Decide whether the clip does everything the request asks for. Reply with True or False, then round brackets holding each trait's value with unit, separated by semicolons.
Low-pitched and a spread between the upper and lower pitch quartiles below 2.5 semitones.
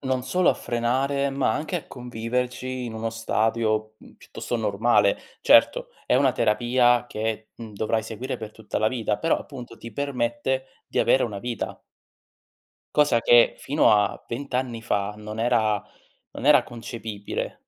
False (120 Hz; 2.8 semitones)